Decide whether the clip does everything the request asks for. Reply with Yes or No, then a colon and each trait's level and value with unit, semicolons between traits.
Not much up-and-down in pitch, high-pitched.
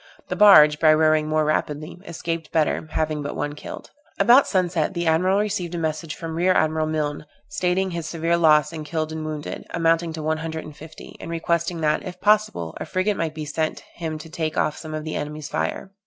No: narrow, 1.8 semitones; medium, 160 Hz